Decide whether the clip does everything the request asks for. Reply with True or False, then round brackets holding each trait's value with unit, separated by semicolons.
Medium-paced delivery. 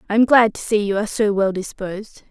False (260 wpm)